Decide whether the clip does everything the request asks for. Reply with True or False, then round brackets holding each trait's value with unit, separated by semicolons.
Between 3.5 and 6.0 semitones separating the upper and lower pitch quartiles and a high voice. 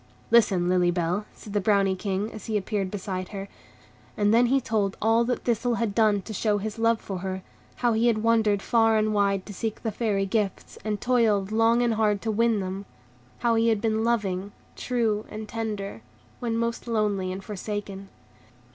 False (2.4 semitones; 215 Hz)